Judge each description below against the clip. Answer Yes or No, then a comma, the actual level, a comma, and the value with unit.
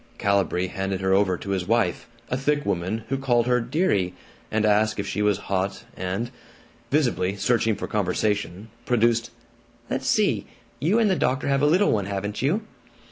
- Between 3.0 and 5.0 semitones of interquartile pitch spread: Yes, average, 4.5 semitones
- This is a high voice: No, low, 110 Hz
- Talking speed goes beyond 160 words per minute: Yes, average, 175 wpm